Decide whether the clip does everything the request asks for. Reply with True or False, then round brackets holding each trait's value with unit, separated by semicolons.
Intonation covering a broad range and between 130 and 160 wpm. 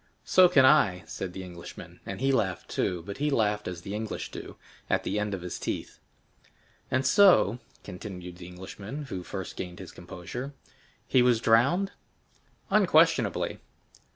True (6.4 semitones; 155 wpm)